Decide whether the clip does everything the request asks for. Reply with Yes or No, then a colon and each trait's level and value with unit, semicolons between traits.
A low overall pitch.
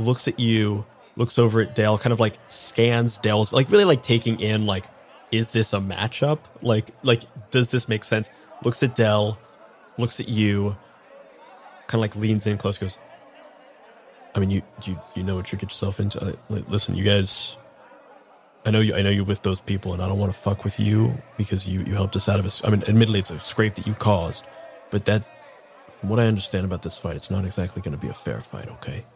Yes: low, 105 Hz